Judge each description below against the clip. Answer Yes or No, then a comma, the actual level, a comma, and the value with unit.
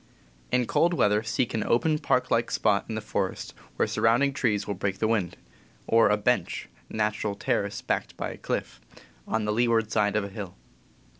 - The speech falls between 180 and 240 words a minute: Yes, average, 190 wpm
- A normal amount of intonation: No, narrow, 2.1 semitones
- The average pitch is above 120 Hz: No, low, 110 Hz